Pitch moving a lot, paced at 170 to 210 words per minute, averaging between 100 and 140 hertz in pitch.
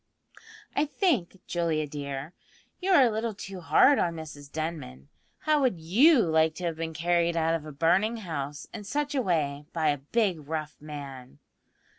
No: wide, 5.9 semitones; average, 175 wpm; medium, 165 Hz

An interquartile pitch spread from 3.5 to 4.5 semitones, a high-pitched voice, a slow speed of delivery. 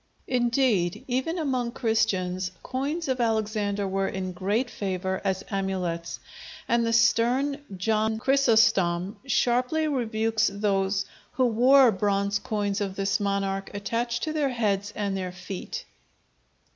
Yes: average, 4.0 semitones; high, 215 Hz; slow, 125 wpm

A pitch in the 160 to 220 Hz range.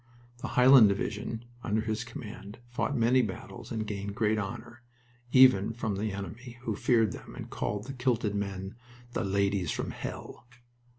No: low, 110 Hz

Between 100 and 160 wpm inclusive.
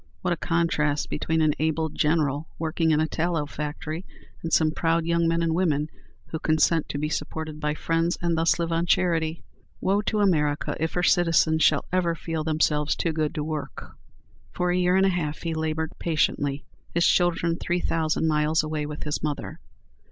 No: average, 190 wpm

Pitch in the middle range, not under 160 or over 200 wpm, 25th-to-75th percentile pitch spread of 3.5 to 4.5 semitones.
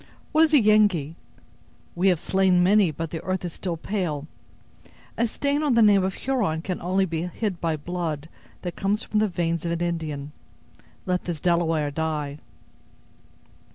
Yes: medium, 175 Hz; average, 170 wpm; average, 3.8 semitones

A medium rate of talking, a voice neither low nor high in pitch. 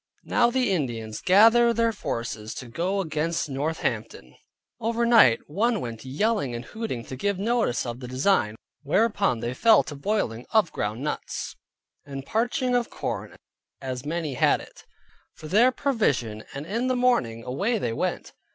Yes: average, 165 wpm; medium, 165 Hz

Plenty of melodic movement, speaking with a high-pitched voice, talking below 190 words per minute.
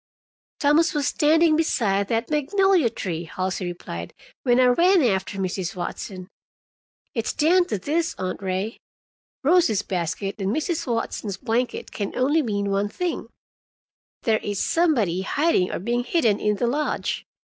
Yes: wide, 7.7 semitones; high, 230 Hz; average, 145 wpm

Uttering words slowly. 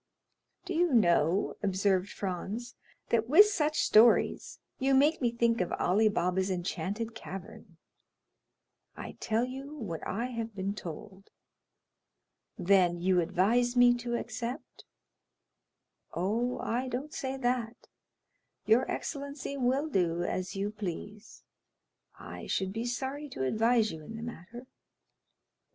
Yes: slow, 125 wpm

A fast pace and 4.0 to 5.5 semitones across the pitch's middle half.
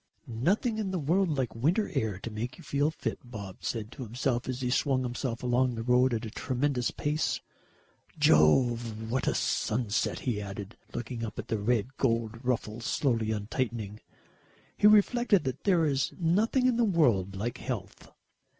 No: average, 170 wpm; average, 4.4 semitones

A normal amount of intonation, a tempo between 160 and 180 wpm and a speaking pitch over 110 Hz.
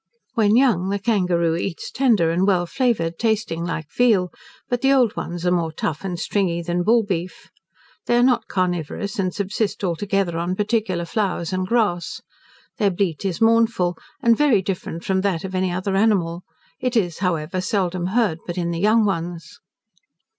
Yes: average, 3.9 semitones; average, 170 wpm; high, 190 Hz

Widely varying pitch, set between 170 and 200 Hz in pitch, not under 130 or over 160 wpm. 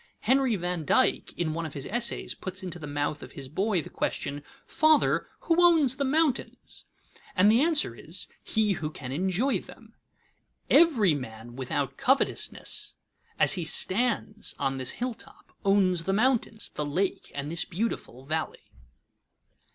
Yes: wide, 8.4 semitones; medium, 185 Hz; average, 150 wpm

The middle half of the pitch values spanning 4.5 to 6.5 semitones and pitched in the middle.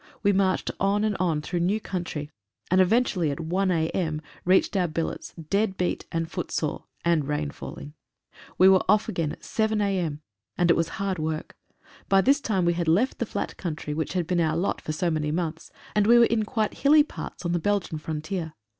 No: average, 3.8 semitones; medium, 175 Hz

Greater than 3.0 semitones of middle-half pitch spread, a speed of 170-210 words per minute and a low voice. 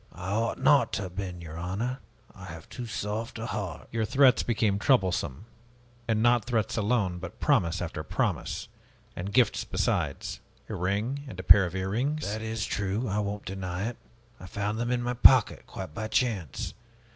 Yes: average, 4.1 semitones; average, 190 wpm; low, 105 Hz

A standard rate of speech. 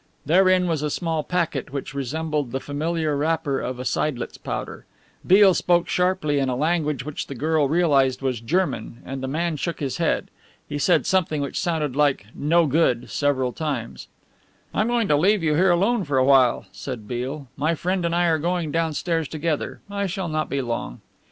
Yes: average, 185 wpm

